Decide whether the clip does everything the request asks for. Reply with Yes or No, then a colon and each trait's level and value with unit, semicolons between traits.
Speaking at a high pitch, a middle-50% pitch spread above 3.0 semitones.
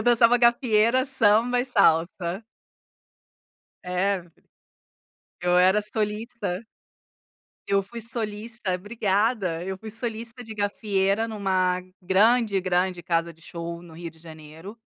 Yes: high, 200 Hz; average, 4.1 semitones